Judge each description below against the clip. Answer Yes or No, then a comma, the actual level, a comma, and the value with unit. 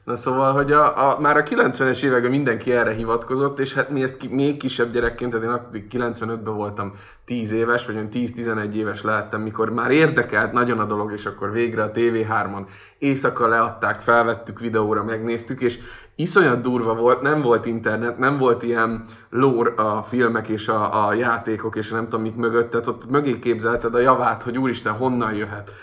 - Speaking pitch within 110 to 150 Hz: Yes, low, 115 Hz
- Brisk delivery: Yes, fast, 185 wpm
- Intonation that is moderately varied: No, narrow, 2.1 semitones